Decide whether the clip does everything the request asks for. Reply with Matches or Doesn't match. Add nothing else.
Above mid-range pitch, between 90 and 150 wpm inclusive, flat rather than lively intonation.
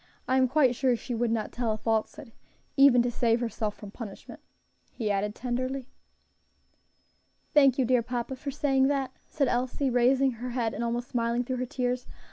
Doesn't match